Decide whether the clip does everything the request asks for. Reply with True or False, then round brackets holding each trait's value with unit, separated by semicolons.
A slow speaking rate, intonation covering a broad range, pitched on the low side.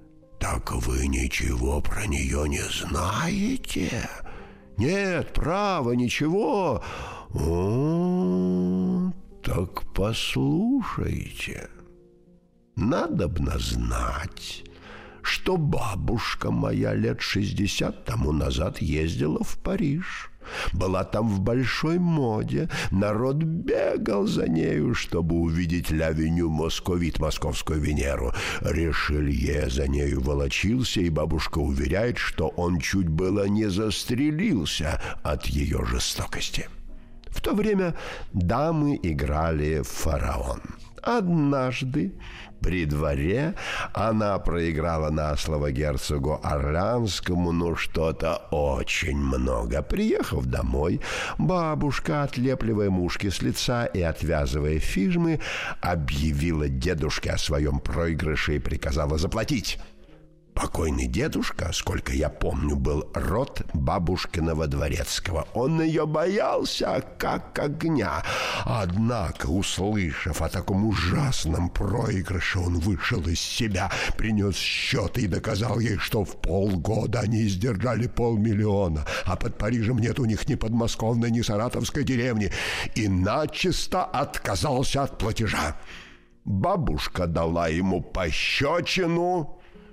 True (100 wpm; 7.5 semitones; 95 Hz)